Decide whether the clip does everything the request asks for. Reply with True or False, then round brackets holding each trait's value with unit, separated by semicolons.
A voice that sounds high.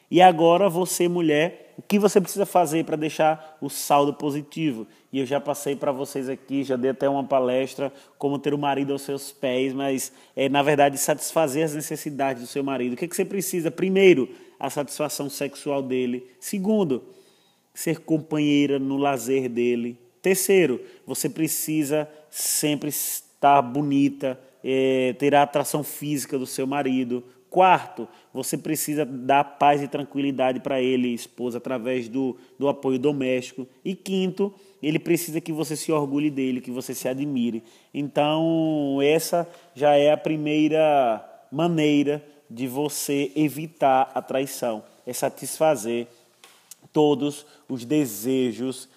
False (145 Hz)